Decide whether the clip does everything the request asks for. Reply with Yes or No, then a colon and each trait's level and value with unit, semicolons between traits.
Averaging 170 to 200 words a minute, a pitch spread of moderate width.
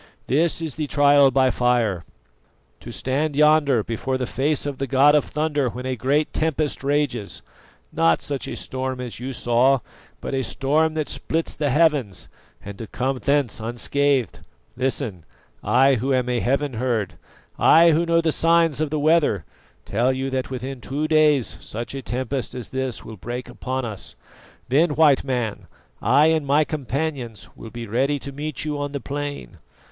Yes: average, 175 wpm; average, 3.2 semitones